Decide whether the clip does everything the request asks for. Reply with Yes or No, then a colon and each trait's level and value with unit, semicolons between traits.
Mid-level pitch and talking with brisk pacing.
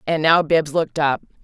Yes: medium, 155 Hz; fast, 210 wpm